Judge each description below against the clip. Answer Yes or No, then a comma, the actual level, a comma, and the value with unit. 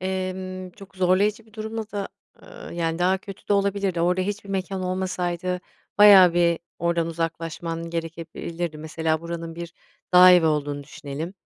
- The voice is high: No, medium, 180 Hz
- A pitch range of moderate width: No, narrow, 2.3 semitones